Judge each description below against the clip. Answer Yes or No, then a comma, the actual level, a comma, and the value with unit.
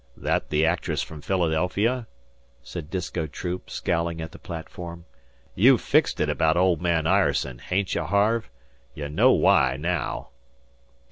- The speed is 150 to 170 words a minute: No, average, 140 wpm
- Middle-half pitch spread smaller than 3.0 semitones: Yes, narrow, 2.6 semitones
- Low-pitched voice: Yes, very low, 85 Hz